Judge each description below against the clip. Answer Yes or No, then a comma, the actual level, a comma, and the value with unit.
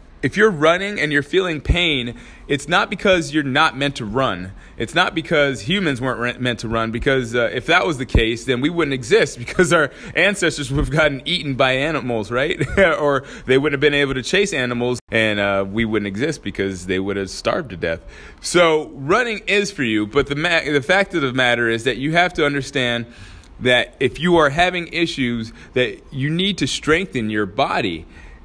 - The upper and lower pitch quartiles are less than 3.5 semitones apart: No, wide, 5.6 semitones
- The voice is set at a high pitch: No, medium, 140 Hz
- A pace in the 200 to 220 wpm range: Yes, fast, 205 wpm